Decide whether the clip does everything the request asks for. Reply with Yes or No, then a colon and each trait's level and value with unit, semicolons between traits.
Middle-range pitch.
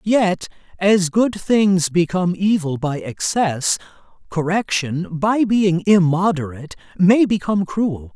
Yes: medium, 180 Hz